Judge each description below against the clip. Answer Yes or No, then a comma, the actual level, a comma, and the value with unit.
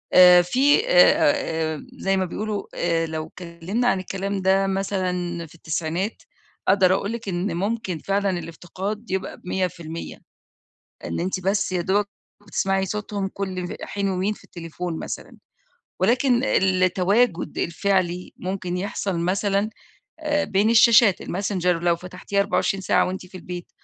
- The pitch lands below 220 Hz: Yes, high, 190 Hz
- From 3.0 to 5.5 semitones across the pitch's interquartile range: No, narrow, 2.4 semitones